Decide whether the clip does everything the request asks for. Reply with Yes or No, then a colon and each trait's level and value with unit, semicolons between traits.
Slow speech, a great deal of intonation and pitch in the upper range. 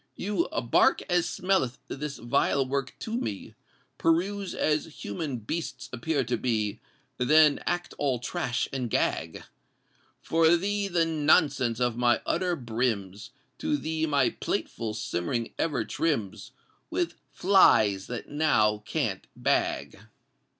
No: slow, 125 wpm; wide, 6.1 semitones; medium, 140 Hz